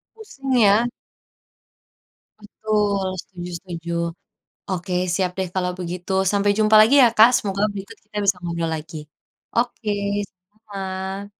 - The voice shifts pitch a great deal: No, average, 3.0 semitones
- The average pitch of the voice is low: No, high, 200 Hz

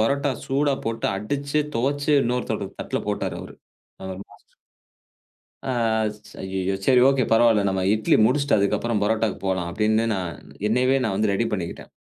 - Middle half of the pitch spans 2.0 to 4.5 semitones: No, average, 5.0 semitones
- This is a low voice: Yes, low, 110 Hz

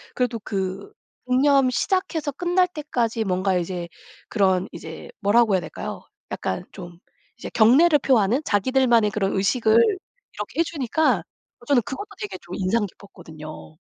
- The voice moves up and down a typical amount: No, wide, 6.6 semitones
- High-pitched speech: Yes, high, 225 Hz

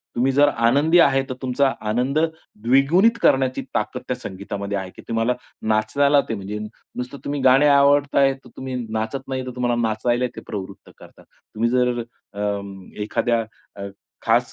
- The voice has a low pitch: Yes, low, 125 Hz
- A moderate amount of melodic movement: Yes, average, 3.8 semitones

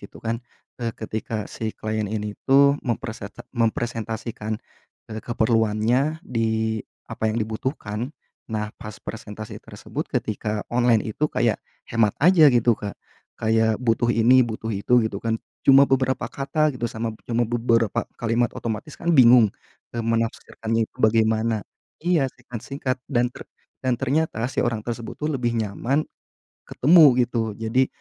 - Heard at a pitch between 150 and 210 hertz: No, low, 115 Hz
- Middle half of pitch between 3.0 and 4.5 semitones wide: No, narrow, 2.4 semitones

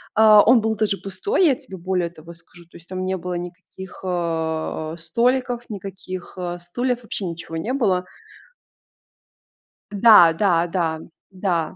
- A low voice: No, medium, 185 Hz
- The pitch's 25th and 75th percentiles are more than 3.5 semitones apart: Yes, average, 4.1 semitones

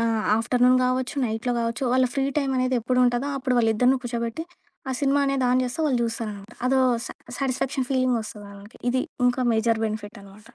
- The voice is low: No, high, 245 Hz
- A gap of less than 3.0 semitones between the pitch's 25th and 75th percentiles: Yes, narrow, 2.4 semitones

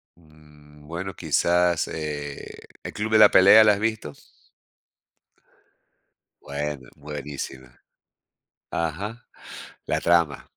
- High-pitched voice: No, very low, 80 Hz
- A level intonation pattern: No, average, 4.6 semitones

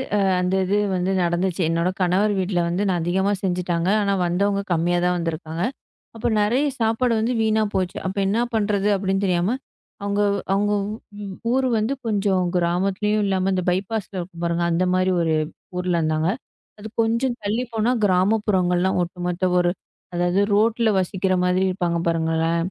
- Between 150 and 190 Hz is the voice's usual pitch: Yes, medium, 185 Hz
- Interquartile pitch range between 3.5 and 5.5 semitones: No, average, 2.8 semitones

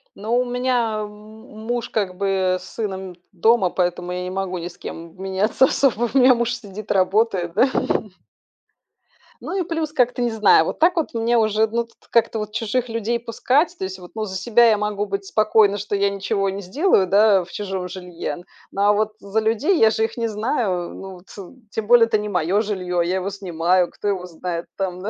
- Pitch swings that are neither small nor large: Yes, average, 3.6 semitones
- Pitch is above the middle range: Yes, high, 210 Hz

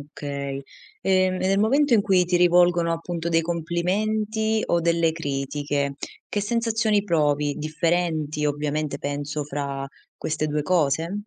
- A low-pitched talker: No, medium, 165 Hz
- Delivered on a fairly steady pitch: No, average, 4.2 semitones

